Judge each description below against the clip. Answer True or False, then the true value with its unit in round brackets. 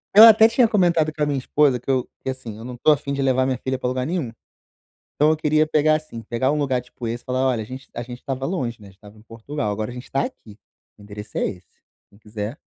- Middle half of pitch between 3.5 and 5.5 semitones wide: True (4.6 semitones)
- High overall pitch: False (130 Hz)